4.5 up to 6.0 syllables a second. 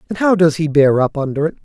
No: 6.4 syllables/s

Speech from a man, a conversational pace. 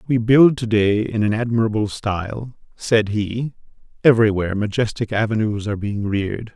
Yes: male; average, 145 wpm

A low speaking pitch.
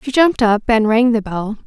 No: high, 230 Hz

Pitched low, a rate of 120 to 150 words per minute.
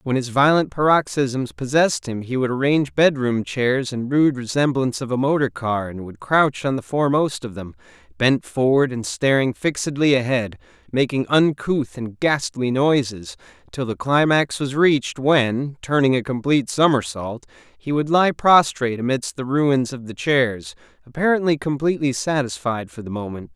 No: low, 130 Hz; average, 160 wpm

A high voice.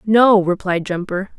Yes: high, 195 Hz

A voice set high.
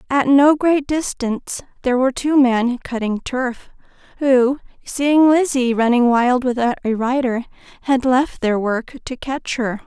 Yes: very high, 255 Hz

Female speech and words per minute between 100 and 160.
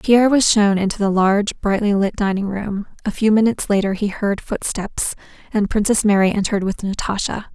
No: female; average, 185 wpm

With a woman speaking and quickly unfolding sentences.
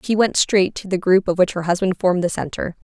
Yes: female; fast, 270 wpm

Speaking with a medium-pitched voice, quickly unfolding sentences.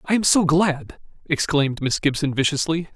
No: medium, 155 Hz; average, 160 wpm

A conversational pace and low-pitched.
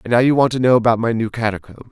No: fast, 315 wpm; low, 115 Hz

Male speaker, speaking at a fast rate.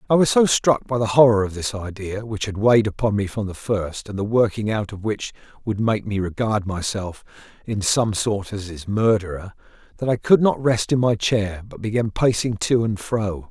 Yes: male; fast, 220 wpm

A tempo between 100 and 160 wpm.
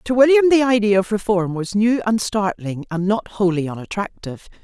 No: average, 180 wpm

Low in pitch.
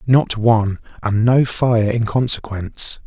Yes: low, 115 Hz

